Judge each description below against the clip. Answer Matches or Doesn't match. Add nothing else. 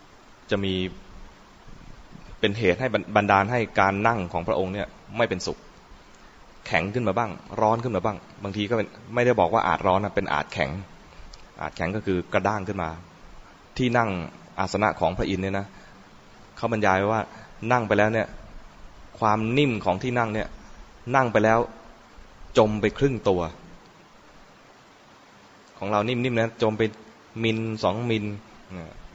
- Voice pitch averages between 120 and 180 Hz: Doesn't match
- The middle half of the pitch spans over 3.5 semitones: Doesn't match